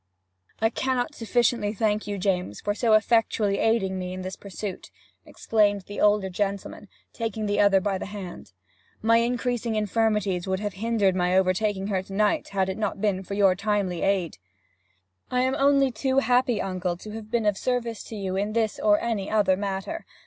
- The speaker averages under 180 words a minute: No, average, 185 wpm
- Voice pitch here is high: Yes, high, 205 Hz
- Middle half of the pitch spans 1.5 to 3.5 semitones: Yes, average, 2.8 semitones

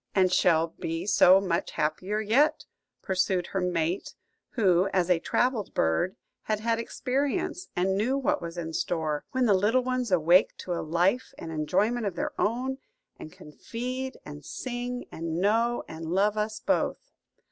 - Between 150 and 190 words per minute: Yes, average, 165 wpm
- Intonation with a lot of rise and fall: Yes, wide, 6.0 semitones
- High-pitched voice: Yes, high, 195 Hz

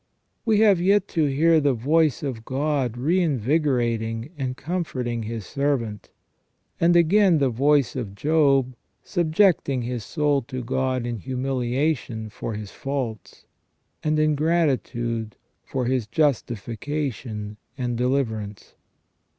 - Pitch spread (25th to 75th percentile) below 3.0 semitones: No, average, 4.6 semitones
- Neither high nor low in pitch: No, low, 130 Hz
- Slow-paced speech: Yes, slow, 120 wpm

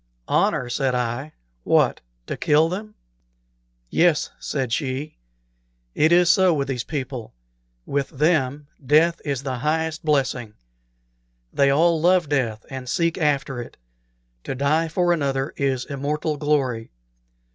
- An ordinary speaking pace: No, slow, 130 wpm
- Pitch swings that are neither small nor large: Yes, average, 3.3 semitones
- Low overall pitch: No, medium, 145 Hz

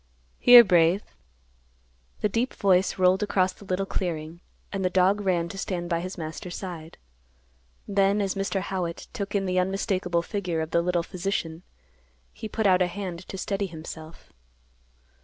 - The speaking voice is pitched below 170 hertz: No, medium, 185 Hz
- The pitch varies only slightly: Yes, narrow, 2.3 semitones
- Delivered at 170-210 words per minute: No, average, 160 wpm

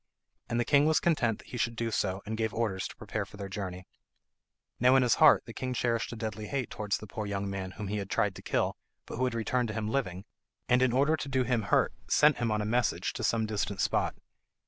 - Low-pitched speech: Yes, low, 115 Hz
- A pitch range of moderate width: Yes, average, 3.4 semitones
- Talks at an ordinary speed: No, fast, 255 wpm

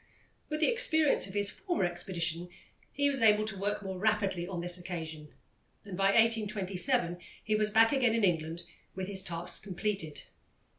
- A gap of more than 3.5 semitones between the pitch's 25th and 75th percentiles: Yes, average, 3.9 semitones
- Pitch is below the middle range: No, high, 195 Hz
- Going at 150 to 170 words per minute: Yes, average, 165 wpm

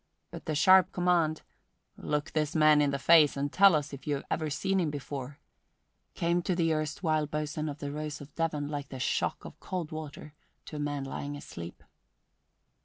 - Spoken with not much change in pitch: Yes, narrow, 2.0 semitones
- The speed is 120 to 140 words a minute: No, average, 190 wpm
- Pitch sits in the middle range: Yes, medium, 150 Hz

